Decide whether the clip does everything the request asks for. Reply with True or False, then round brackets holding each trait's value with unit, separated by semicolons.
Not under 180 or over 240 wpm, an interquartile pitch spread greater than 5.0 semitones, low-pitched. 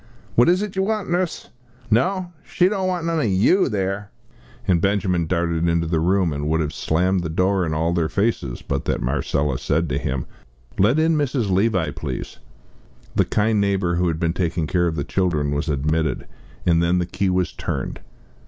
True (195 wpm; 5.4 semitones; 90 Hz)